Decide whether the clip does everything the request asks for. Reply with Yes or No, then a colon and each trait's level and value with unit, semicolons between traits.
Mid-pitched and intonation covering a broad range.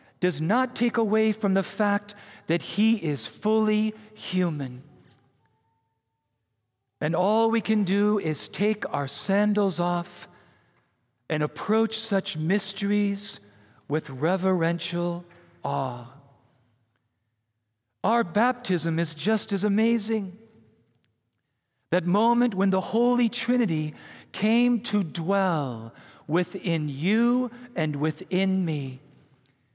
Yes: medium, 175 Hz; wide, 7.9 semitones